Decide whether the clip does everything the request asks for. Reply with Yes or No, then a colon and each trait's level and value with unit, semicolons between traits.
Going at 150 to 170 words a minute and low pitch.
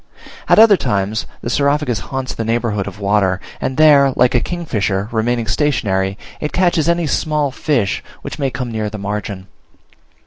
Yes: average, 165 wpm; low, 120 Hz